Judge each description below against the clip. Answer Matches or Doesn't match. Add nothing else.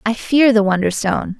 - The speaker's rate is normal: Matches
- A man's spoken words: Doesn't match